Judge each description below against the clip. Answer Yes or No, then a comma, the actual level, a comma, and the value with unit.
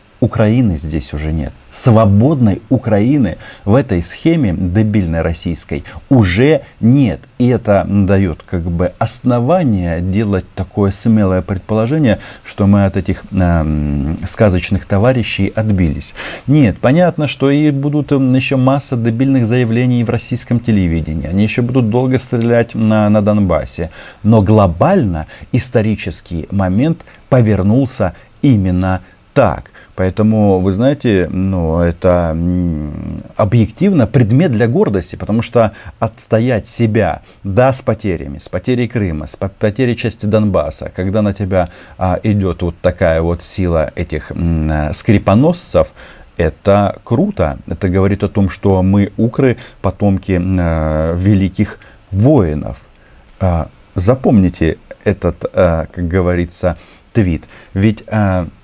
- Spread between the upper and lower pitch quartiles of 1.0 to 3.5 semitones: No, average, 4.6 semitones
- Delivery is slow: No, average, 120 wpm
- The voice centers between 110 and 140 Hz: No, low, 100 Hz